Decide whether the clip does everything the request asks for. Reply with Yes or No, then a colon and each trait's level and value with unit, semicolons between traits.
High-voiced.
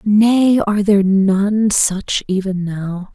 Yes: high, 200 Hz